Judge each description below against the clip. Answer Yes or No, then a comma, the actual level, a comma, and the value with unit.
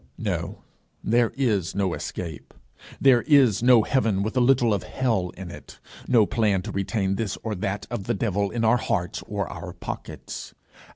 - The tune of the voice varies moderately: Yes, average, 3.7 semitones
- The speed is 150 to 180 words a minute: Yes, average, 175 wpm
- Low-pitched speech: Yes, low, 110 Hz